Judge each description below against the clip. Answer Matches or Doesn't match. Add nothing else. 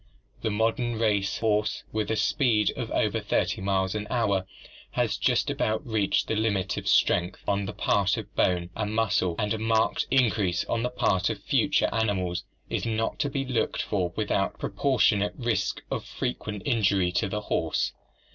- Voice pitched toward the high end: Doesn't match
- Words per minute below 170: Doesn't match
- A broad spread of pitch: Doesn't match